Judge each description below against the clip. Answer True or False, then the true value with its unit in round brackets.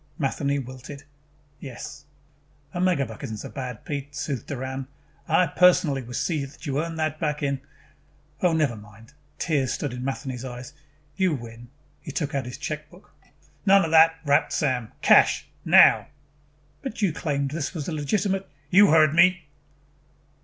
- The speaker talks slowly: False (160 wpm)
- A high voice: False (145 Hz)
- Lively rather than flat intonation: False (3.7 semitones)